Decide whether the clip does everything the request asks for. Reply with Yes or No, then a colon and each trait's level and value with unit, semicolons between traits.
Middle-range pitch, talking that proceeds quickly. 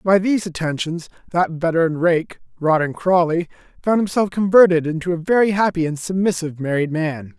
No: medium, 170 Hz; average, 155 wpm